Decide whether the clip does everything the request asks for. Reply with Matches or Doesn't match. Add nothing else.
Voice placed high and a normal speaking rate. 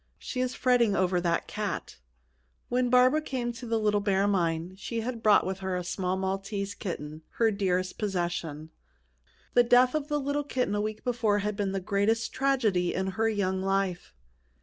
Matches